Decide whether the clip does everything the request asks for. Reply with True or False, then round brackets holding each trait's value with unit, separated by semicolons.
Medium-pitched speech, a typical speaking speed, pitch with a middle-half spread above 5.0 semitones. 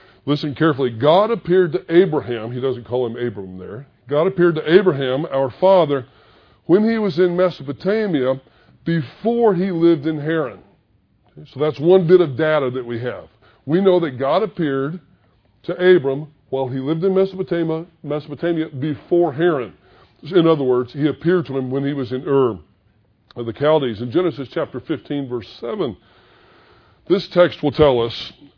True (145 Hz; 160 wpm; 5.5 semitones)